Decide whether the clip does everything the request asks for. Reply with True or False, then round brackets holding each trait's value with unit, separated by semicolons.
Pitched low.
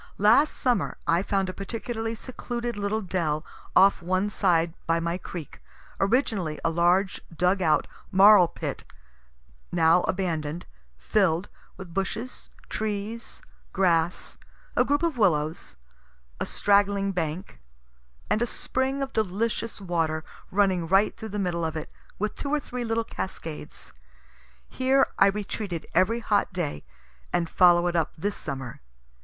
False (190 Hz)